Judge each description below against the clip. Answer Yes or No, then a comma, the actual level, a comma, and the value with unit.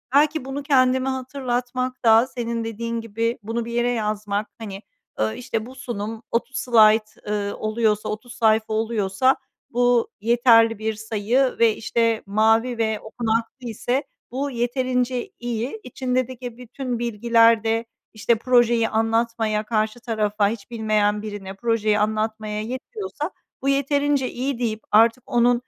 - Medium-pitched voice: No, high, 230 Hz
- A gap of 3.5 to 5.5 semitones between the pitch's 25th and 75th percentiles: No, narrow, 2.4 semitones